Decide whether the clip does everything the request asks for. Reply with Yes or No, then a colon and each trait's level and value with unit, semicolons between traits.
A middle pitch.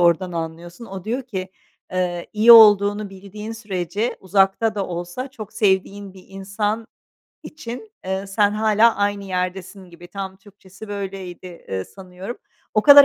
No: high, 195 Hz